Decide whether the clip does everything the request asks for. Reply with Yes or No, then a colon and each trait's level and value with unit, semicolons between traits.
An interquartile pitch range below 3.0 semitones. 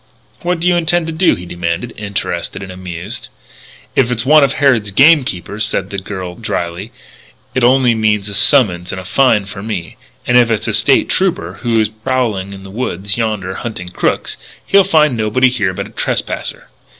No: average, 5.3 semitones